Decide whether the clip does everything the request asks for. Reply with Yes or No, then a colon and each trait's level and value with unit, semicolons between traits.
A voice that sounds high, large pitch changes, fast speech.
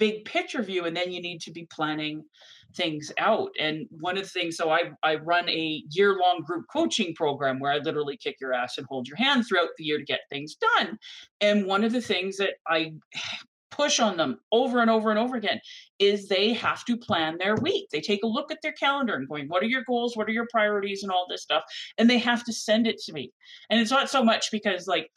Yes: high, 200 Hz; wide, 6.2 semitones; fast, 245 wpm